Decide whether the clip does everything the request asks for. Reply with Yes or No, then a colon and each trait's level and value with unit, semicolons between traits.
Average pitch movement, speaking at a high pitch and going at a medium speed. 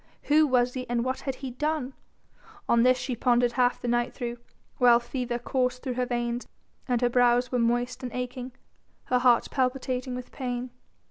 No: narrow, 0.9 semitones; very high, 250 Hz; average, 185 wpm